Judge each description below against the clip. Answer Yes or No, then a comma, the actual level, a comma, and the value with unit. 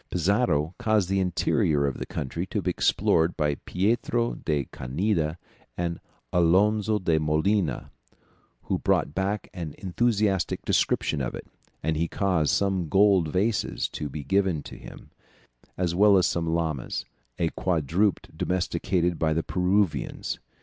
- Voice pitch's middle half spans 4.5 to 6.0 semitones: No, average, 4.0 semitones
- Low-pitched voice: Yes, very low, 90 Hz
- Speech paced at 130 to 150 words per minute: Yes, average, 145 wpm